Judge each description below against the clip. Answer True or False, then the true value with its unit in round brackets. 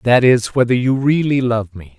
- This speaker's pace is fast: True (210 wpm)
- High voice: False (120 Hz)